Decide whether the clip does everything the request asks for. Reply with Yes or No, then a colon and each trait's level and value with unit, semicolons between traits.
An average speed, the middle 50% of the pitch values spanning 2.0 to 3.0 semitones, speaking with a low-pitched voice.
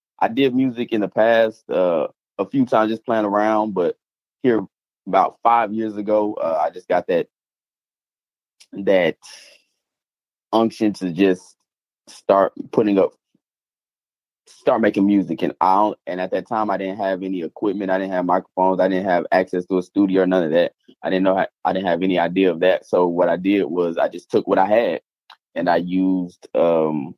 Yes: average, 190 wpm; average, 2.7 semitones; very low, 95 Hz